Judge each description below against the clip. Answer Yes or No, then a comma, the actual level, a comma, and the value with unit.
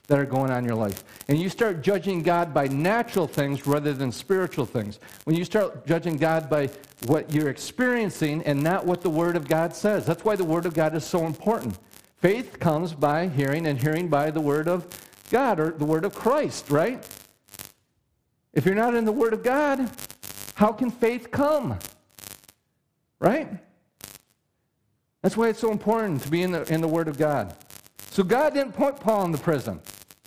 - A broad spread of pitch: Yes, wide, 5.9 semitones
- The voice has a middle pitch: Yes, medium, 165 Hz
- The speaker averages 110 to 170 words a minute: No, average, 190 wpm